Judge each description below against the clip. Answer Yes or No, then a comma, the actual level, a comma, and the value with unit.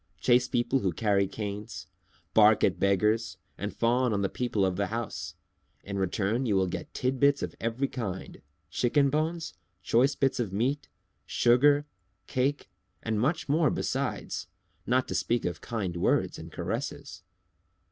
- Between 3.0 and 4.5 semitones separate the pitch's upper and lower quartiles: No, average, 5.1 semitones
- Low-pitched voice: Yes, low, 115 Hz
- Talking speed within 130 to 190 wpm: Yes, average, 150 wpm